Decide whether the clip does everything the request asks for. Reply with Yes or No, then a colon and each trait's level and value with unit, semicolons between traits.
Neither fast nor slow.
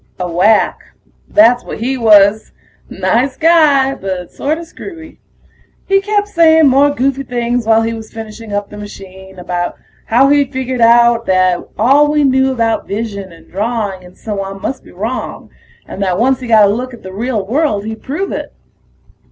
Yes: average, 175 wpm